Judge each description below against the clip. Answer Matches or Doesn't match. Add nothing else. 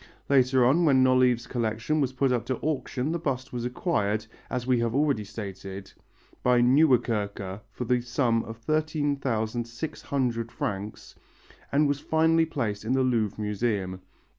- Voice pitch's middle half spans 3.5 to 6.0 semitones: Matches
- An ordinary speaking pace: Matches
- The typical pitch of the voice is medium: Doesn't match